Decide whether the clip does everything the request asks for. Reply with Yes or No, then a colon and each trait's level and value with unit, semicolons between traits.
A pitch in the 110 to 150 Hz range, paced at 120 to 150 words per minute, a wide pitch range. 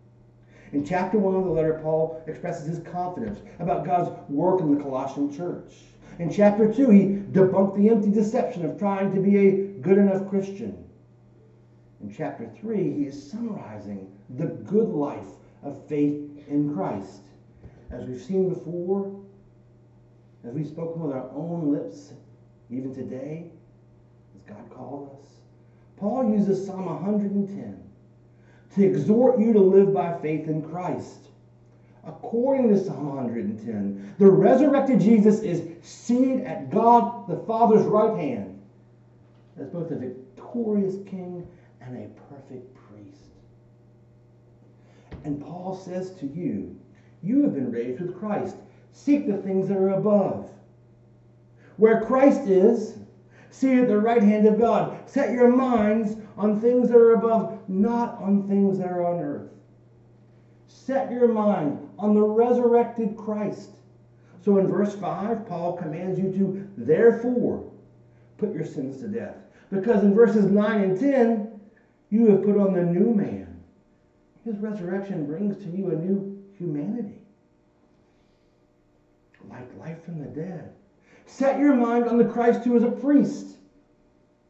No: medium, 185 Hz; average, 140 wpm; wide, 7.7 semitones